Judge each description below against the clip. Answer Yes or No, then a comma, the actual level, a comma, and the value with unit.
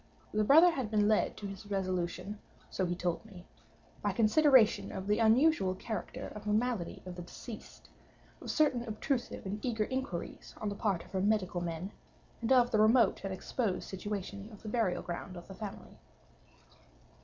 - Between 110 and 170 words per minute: No, average, 180 wpm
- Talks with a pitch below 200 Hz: No, high, 210 Hz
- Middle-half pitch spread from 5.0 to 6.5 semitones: No, average, 3.4 semitones